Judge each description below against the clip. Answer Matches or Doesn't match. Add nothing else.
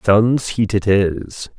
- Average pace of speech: Matches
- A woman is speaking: Doesn't match